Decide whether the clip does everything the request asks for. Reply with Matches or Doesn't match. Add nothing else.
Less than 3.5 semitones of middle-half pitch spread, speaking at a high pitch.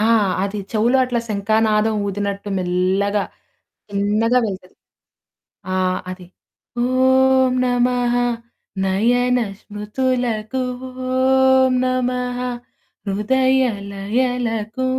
Doesn't match